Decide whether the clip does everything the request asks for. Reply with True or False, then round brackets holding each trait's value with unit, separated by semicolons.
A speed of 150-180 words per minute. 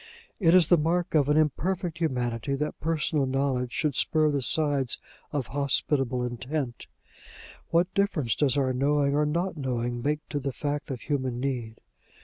True (160 wpm)